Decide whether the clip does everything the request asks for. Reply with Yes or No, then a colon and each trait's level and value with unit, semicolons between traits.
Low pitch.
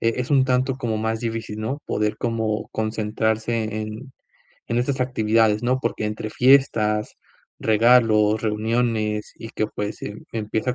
Yes: low, 110 Hz